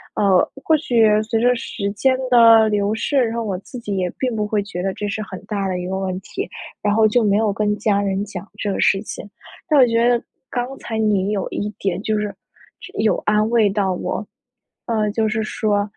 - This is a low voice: No, high, 210 Hz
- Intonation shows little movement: Yes, narrow, 2.2 semitones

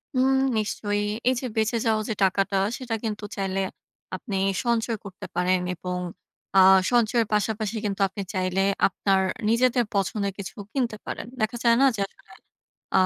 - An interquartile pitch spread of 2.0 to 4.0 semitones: Yes, average, 3.1 semitones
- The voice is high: Yes, high, 210 Hz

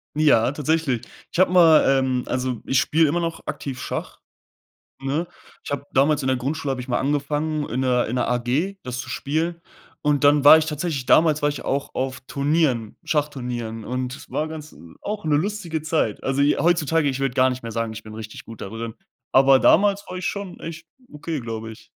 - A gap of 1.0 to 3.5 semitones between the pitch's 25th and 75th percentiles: No, average, 3.9 semitones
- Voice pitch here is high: No, medium, 145 Hz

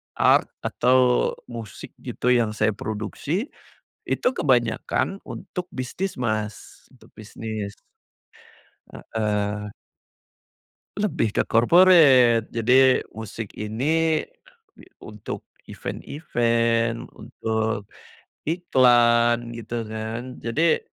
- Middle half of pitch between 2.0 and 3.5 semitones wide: Yes, average, 2.9 semitones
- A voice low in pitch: Yes, low, 115 Hz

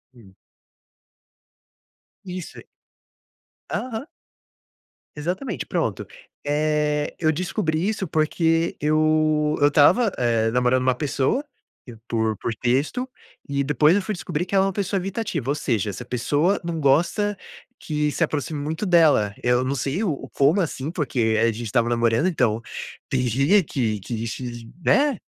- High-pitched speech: No, medium, 150 Hz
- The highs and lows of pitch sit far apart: Yes, wide, 6.0 semitones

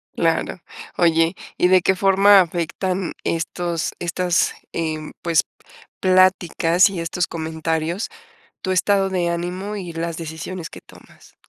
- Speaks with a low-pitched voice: No, medium, 175 Hz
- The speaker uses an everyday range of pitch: No, narrow, 2.2 semitones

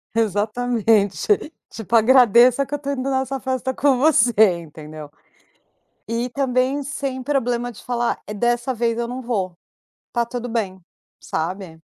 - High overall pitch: Yes, high, 240 Hz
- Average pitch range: Yes, average, 3.5 semitones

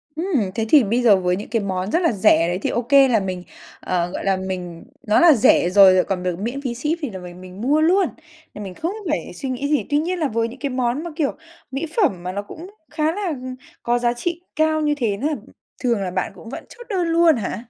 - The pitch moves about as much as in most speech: No, wide, 8.1 semitones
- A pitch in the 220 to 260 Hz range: Yes, high, 240 Hz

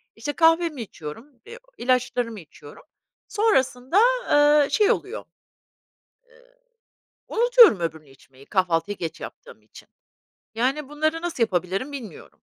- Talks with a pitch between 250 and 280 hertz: Yes, very high, 265 Hz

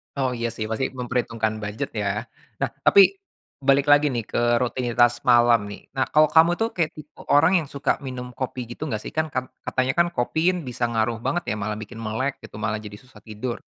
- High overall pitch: No, low, 125 Hz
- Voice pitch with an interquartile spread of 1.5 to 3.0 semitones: No, average, 4.3 semitones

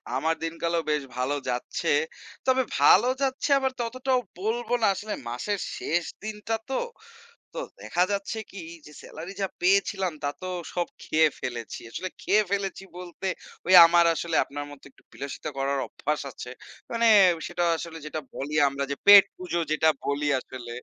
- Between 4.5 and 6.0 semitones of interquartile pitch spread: Yes, wide, 5.6 semitones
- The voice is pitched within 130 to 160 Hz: No, medium, 175 Hz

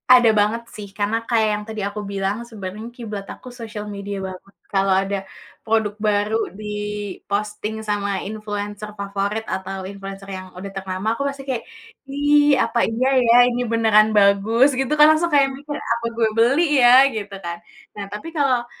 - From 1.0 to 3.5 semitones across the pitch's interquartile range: Yes, average, 3.0 semitones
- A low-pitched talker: No, high, 210 Hz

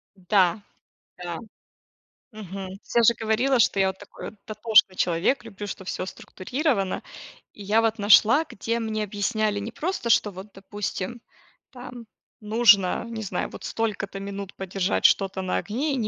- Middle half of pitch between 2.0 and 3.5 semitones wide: Yes, average, 2.9 semitones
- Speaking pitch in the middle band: No, high, 210 Hz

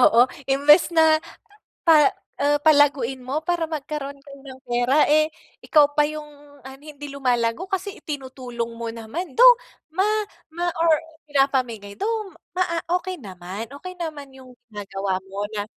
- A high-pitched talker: Yes, very high, 285 Hz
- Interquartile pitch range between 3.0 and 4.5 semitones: Yes, average, 4.1 semitones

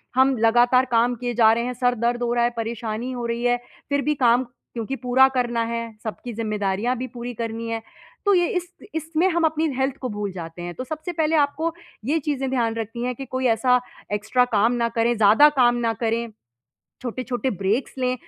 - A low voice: No, high, 245 Hz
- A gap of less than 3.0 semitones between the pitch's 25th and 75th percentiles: Yes, narrow, 2.6 semitones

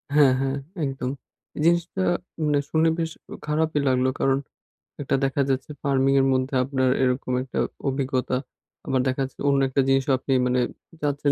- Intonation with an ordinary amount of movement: No, narrow, 1.9 semitones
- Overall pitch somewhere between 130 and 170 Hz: Yes, low, 135 Hz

